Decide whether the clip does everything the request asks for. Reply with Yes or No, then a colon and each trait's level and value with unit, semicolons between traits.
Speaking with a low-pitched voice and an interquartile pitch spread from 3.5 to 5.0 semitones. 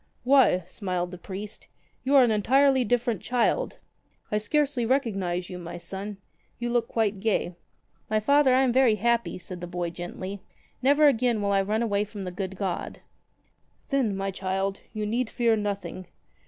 No: high, 210 Hz; average, 4.3 semitones